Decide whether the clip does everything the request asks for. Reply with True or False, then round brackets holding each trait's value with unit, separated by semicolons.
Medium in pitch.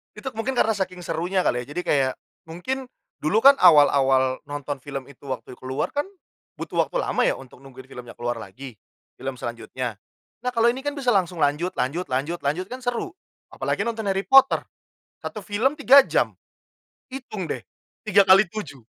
True (175 Hz)